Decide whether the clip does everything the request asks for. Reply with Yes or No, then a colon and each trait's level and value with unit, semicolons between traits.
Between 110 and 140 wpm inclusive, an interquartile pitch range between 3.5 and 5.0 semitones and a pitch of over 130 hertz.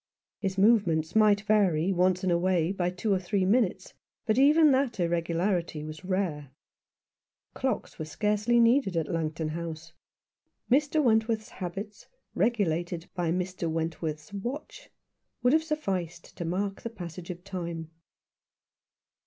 Yes: slow, 135 wpm; average, 4.4 semitones; medium, 185 Hz